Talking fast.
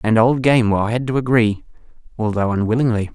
No: average, 150 wpm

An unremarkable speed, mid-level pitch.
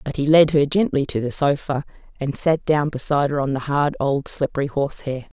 No: fast, 210 wpm; medium, 145 Hz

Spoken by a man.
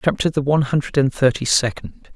Yes: male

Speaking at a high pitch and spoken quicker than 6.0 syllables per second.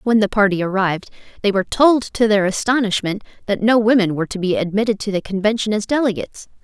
Yes: high, 210 Hz; 6.5 syllables/s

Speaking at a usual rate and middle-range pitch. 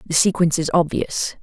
Yes: average, 170 wpm; medium, 165 Hz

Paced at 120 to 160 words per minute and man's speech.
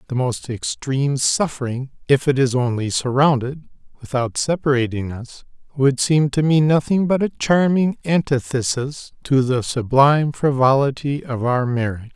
Yes: average, 140 wpm; male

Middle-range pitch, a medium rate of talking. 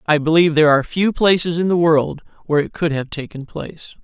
No: medium, 160 Hz; fast, 225 wpm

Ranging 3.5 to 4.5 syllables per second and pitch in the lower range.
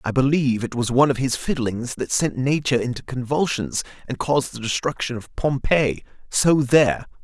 No: 5.4 syllables/s; low, 130 Hz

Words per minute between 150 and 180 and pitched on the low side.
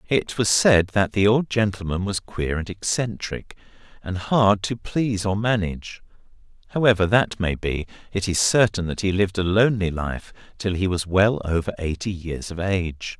Yes: average, 175 wpm; low, 100 Hz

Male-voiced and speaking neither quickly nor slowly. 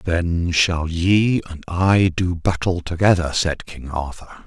Yes: male; average, 150 wpm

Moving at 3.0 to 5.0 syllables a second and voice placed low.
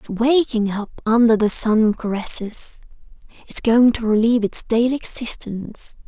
No: 4.7 syllables/s; high, 225 Hz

